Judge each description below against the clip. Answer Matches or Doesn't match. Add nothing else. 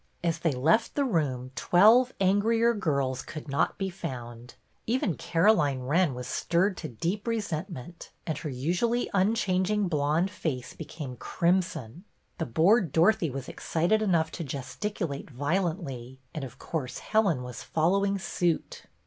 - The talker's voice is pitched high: Doesn't match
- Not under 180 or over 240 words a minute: Doesn't match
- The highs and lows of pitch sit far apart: Matches